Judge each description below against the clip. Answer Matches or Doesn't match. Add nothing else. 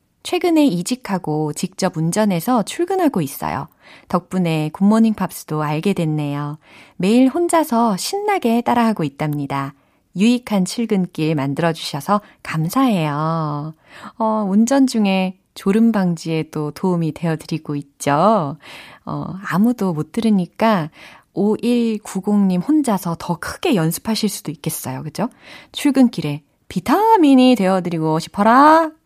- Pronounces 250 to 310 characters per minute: Matches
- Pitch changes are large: Matches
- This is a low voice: Doesn't match